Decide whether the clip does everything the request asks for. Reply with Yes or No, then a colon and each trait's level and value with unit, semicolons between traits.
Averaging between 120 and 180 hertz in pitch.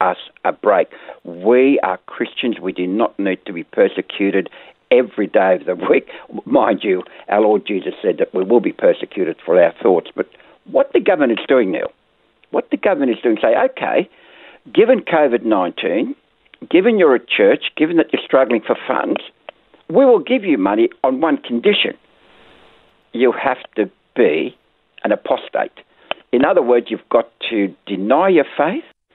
Yes: low, 135 Hz